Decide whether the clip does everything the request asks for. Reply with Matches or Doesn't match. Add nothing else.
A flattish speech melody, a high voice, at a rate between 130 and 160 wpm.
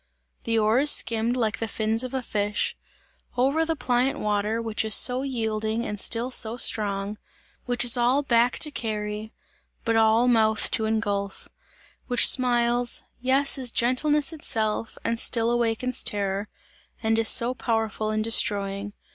Matches